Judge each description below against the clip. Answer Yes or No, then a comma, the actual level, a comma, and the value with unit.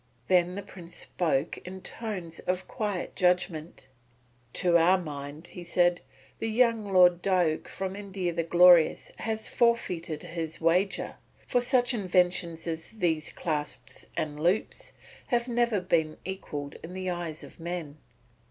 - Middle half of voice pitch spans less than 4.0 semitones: Yes, average, 2.8 semitones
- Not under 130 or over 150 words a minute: Yes, average, 140 wpm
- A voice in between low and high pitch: Yes, medium, 180 Hz